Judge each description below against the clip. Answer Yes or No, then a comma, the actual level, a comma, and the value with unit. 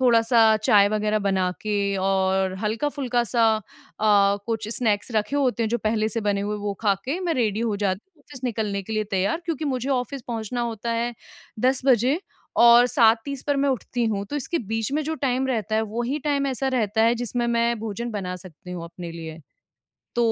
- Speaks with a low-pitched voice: No, high, 230 Hz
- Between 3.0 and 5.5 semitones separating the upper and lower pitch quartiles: Yes, average, 3.4 semitones